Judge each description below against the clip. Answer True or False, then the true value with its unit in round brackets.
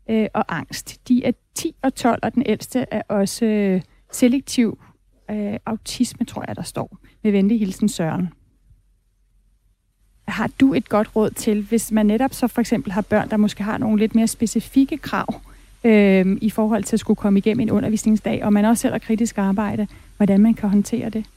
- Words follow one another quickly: False (185 wpm)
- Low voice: False (215 Hz)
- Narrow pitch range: True (2.2 semitones)